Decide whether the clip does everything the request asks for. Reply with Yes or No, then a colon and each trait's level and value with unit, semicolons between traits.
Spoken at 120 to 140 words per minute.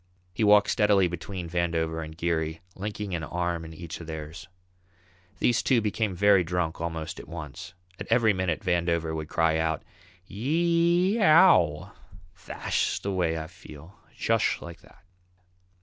No: average, 150 wpm